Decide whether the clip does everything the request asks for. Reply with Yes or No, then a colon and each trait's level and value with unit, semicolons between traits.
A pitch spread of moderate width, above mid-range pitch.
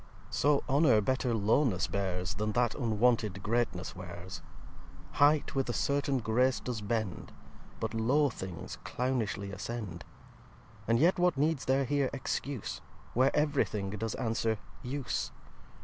No: average, 4.8 semitones; low, 120 Hz